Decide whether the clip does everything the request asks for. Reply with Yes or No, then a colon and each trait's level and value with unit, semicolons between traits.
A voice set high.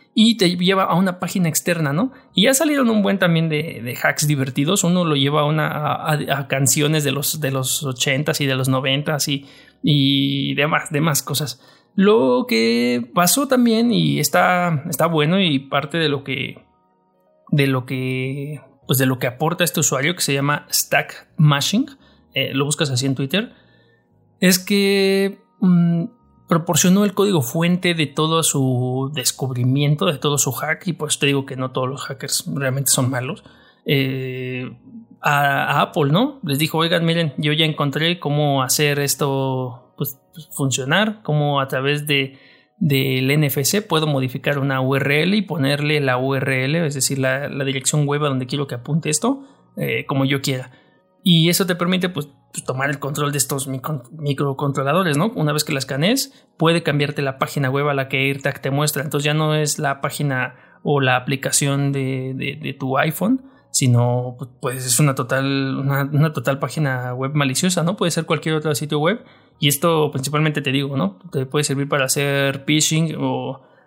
No: medium, 145 Hz